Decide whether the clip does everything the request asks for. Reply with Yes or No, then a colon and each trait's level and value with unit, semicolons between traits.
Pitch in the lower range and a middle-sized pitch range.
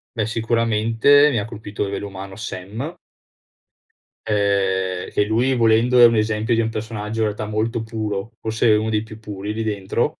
No: low, 110 Hz; narrow, 1.8 semitones